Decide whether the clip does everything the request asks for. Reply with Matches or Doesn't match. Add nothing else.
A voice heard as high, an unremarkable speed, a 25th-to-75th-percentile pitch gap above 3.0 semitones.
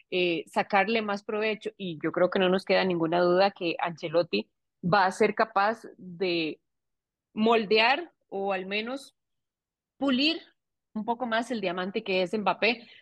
Matches